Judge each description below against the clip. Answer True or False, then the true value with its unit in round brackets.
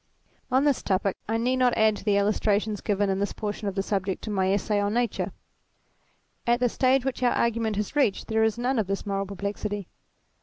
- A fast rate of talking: True (215 wpm)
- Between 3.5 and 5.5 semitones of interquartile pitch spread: False (3.0 semitones)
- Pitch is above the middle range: True (210 Hz)